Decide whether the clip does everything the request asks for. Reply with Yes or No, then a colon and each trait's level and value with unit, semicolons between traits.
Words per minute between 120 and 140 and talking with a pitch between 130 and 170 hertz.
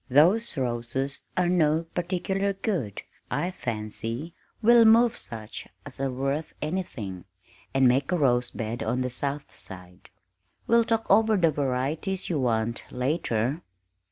Yes: slow, 135 wpm; medium, 140 Hz